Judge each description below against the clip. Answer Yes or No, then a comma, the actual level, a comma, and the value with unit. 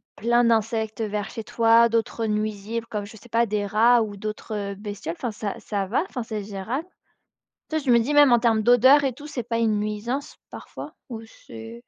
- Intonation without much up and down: Yes, narrow, 2.3 semitones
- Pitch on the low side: No, high, 225 Hz